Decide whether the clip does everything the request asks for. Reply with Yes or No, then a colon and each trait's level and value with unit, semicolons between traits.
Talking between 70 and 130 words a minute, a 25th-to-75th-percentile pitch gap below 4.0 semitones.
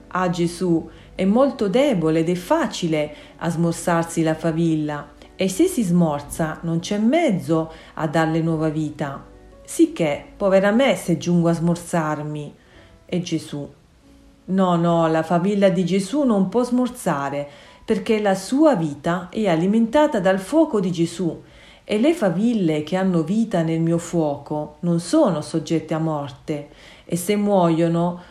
No: average, 145 wpm; average, 3.6 semitones